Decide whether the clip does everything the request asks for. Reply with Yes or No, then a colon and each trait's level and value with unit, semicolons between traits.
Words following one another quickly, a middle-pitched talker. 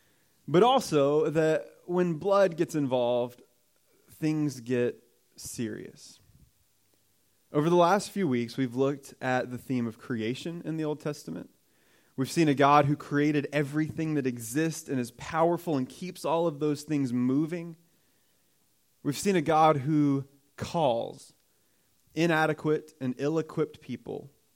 No: slow, 135 wpm; medium, 150 Hz